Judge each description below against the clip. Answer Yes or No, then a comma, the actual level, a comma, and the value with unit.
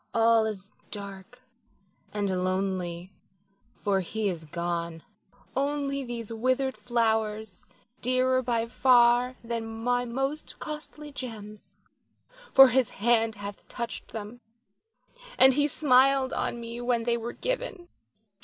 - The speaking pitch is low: No, high, 235 Hz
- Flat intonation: No, average, 3.6 semitones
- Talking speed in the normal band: No, slow, 115 wpm